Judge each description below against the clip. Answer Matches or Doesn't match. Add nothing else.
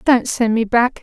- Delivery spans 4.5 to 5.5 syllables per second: Doesn't match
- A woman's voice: Matches